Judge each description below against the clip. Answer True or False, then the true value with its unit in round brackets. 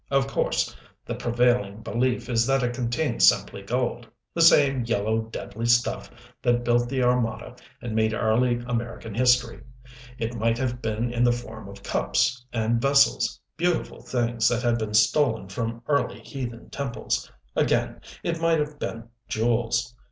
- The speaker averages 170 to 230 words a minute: False (155 wpm)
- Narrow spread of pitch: True (1.9 semitones)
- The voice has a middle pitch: False (120 Hz)